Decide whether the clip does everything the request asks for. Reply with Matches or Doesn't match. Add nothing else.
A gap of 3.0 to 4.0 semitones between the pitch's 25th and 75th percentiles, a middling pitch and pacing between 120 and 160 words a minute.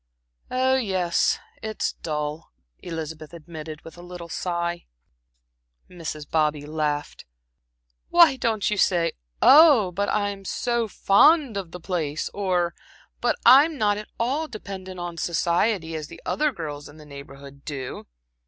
Doesn't match